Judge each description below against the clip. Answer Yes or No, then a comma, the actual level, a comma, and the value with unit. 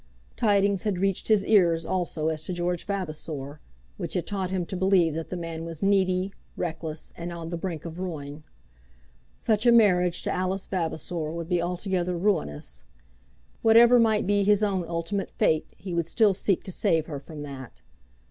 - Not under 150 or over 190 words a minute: Yes, average, 175 wpm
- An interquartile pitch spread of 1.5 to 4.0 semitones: Yes, average, 3.2 semitones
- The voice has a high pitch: No, medium, 180 Hz